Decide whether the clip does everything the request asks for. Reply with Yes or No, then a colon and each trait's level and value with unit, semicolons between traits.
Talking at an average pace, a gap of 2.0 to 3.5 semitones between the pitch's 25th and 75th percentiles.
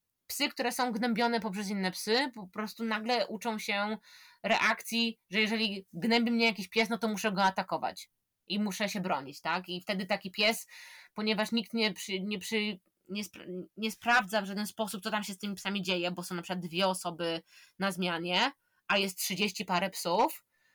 No: fast, 190 wpm; average, 3.0 semitones